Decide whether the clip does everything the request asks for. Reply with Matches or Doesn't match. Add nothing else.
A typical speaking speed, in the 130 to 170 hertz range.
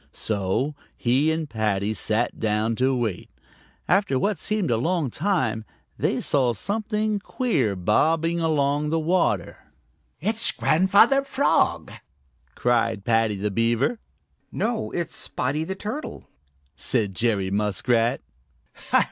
Doesn't match